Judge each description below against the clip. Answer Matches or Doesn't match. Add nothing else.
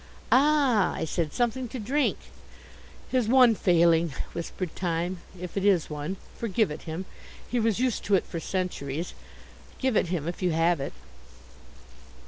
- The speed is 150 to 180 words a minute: Matches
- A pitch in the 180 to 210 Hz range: Matches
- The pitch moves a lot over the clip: Matches